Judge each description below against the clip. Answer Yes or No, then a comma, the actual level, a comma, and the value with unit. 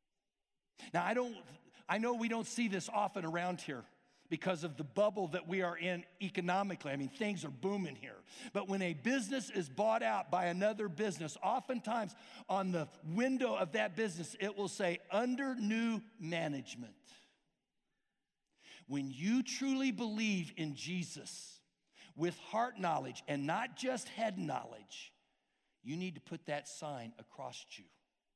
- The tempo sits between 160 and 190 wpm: No, average, 150 wpm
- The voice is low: No, high, 190 Hz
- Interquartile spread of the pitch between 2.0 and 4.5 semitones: No, average, 5.2 semitones